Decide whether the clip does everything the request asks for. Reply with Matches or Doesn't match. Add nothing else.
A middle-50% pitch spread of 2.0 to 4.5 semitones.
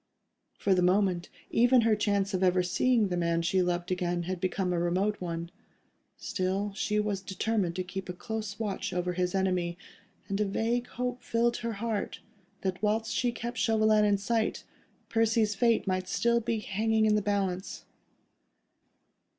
Matches